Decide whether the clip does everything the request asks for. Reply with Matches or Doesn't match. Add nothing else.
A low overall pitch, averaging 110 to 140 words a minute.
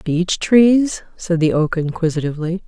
Doesn't match